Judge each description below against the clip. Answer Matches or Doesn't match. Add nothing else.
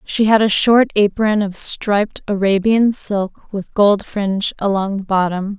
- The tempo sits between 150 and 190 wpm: Matches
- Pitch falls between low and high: Doesn't match